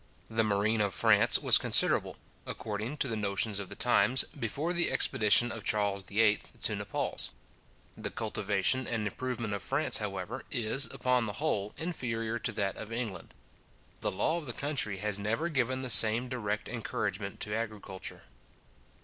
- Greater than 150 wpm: Yes, average, 160 wpm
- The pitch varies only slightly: No, average, 3.4 semitones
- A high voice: No, low, 110 Hz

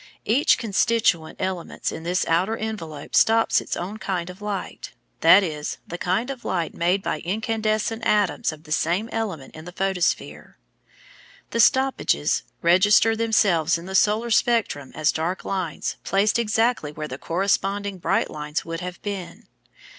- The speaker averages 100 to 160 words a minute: Yes, average, 155 wpm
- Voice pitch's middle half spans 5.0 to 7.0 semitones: No, average, 4.6 semitones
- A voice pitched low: No, high, 190 Hz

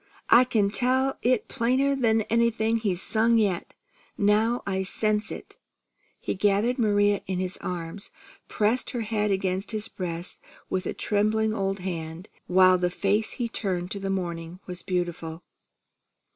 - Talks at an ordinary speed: Yes, average, 145 wpm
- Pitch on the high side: Yes, high, 205 Hz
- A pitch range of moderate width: Yes, average, 3.4 semitones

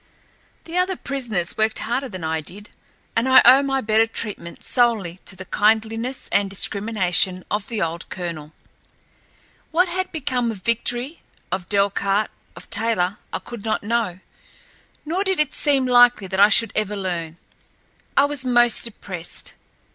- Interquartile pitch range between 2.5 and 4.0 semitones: No, average, 4.8 semitones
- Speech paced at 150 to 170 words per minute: Yes, average, 155 wpm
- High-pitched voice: Yes, high, 220 Hz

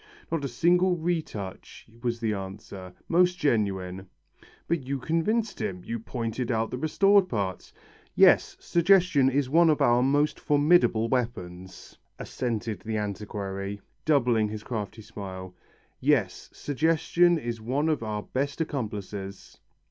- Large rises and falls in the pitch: Yes, wide, 7.1 semitones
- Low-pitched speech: Yes, low, 120 Hz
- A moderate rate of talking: No, slow, 130 wpm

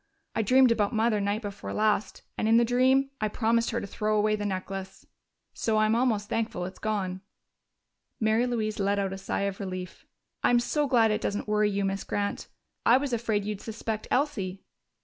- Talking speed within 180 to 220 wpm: Yes, average, 190 wpm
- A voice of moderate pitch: No, high, 215 Hz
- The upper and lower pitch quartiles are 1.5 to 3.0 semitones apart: Yes, narrow, 2.5 semitones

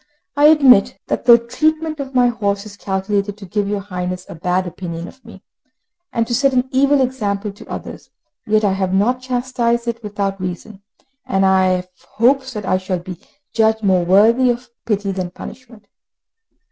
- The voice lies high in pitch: Yes, high, 210 Hz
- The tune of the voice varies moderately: Yes, average, 4.4 semitones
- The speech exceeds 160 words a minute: Yes, average, 180 wpm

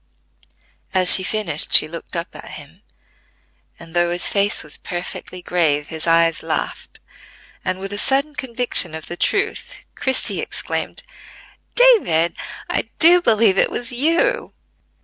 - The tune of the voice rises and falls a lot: Yes, wide, 7.3 semitones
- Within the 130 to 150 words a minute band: Yes, average, 140 wpm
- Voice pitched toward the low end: No, medium, 185 Hz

